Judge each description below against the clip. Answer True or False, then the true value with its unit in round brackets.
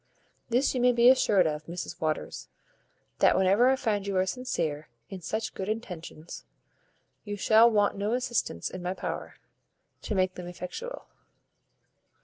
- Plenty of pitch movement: False (4.8 semitones)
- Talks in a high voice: True (200 Hz)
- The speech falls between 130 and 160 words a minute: True (150 wpm)